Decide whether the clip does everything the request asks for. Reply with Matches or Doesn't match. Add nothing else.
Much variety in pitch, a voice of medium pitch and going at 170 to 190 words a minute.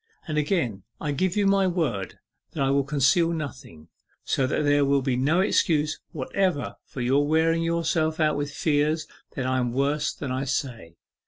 Doesn't match